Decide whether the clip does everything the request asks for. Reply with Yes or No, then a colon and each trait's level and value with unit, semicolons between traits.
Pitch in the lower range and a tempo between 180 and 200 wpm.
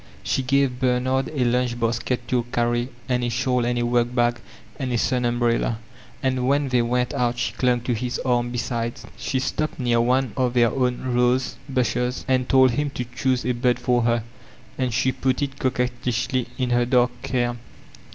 Yes: low, 125 Hz; average, 185 wpm